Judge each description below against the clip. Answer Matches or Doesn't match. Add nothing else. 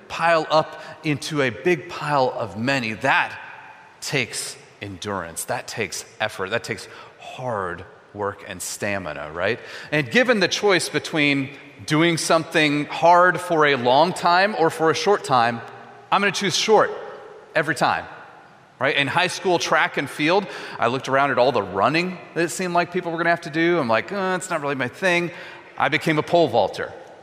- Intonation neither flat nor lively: Matches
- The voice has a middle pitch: Matches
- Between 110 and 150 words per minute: Doesn't match